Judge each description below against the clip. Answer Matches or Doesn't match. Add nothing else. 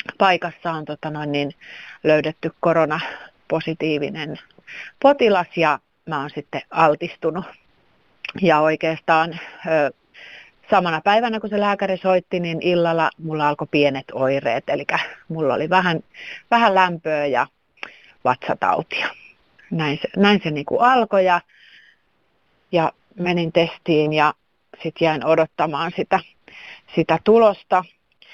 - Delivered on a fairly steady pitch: Doesn't match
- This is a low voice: Doesn't match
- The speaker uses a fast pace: Doesn't match